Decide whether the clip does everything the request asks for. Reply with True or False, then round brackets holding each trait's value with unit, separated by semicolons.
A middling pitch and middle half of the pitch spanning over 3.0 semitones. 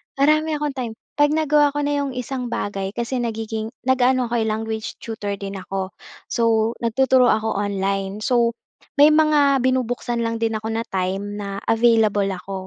False (230 Hz; 4.1 semitones)